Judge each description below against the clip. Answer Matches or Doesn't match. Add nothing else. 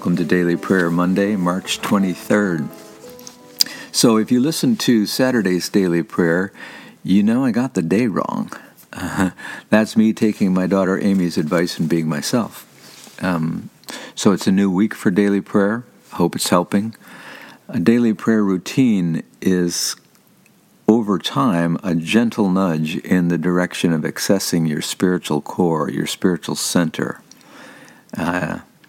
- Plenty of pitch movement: Doesn't match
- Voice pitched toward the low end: Matches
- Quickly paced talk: Doesn't match